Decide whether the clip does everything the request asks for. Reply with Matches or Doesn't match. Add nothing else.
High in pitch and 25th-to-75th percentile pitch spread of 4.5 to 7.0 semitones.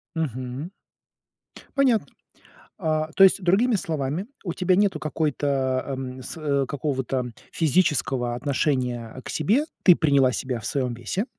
Doesn't match